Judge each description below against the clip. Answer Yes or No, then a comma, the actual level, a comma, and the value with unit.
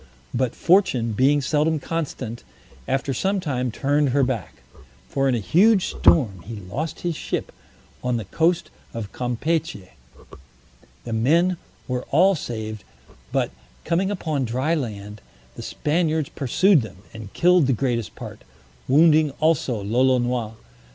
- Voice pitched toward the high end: No, low, 135 Hz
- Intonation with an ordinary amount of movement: No, wide, 5.7 semitones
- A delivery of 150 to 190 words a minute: No, slow, 135 wpm